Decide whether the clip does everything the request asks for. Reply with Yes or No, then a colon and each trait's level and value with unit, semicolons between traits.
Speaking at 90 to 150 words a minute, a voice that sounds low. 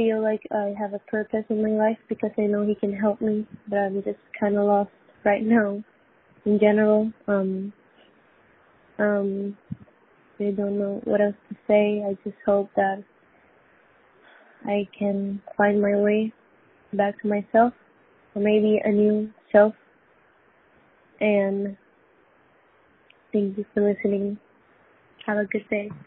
No: average, 145 wpm; high, 210 Hz